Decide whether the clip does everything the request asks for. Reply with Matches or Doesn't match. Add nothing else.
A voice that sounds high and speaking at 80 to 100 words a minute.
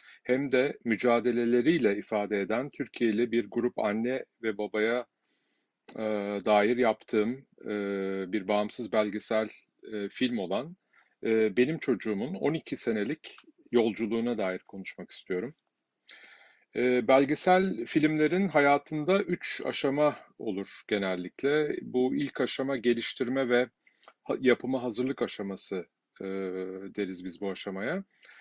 Doesn't match